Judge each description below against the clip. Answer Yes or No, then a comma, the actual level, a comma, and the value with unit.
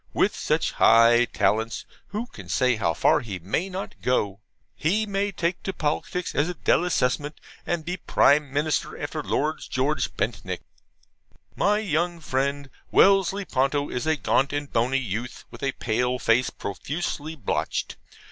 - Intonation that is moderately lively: No, wide, 5.8 semitones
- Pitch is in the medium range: Yes, medium, 145 Hz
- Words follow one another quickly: No, average, 150 wpm